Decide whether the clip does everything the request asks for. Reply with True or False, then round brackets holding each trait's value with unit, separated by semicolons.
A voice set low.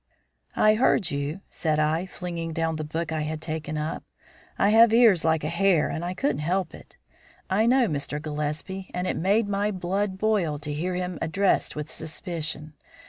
False (170 Hz)